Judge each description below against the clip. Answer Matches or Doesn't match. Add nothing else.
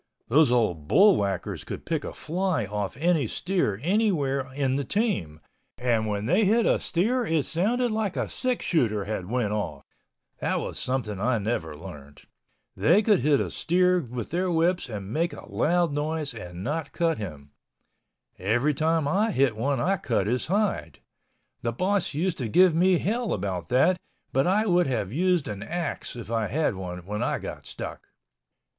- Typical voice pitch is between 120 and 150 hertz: Matches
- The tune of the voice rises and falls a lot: Matches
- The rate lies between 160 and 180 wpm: Matches